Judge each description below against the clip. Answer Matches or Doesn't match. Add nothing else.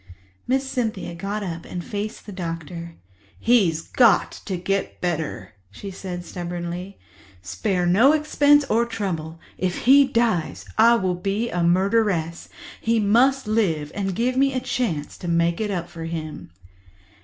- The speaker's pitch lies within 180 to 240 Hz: Matches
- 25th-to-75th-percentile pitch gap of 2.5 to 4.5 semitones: Doesn't match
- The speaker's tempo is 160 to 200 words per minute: Doesn't match